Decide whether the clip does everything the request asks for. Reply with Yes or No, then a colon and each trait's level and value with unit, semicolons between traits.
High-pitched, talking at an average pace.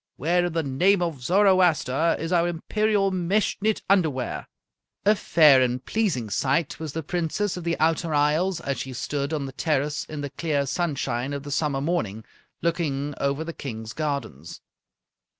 No: medium, 155 Hz; average, 170 wpm